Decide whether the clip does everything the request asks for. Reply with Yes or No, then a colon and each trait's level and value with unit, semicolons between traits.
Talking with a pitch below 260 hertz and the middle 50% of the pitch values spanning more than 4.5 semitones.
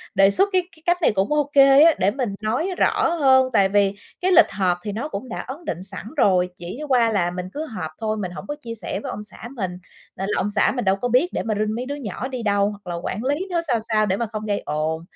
Yes: high, 215 Hz; wide, 5.5 semitones